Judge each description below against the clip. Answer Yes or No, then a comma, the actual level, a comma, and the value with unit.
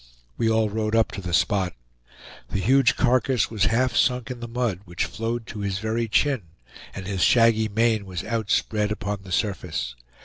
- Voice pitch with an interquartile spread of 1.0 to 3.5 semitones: Yes, average, 3.0 semitones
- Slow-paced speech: No, average, 180 wpm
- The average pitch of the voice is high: No, low, 110 Hz